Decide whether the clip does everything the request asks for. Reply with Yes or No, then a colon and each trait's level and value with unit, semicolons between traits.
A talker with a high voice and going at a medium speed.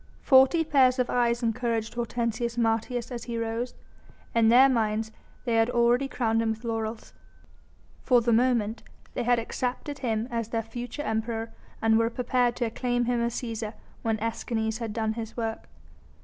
Yes: high, 235 Hz; average, 165 wpm